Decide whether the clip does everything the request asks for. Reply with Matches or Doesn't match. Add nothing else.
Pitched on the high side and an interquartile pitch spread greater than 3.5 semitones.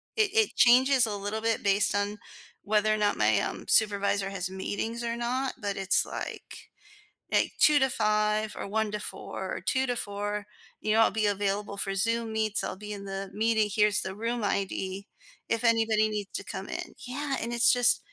Doesn't match